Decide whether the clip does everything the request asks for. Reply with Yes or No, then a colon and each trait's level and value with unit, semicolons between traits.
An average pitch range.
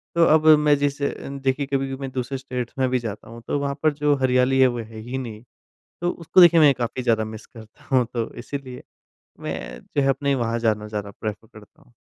Yes: average, 3.5 semitones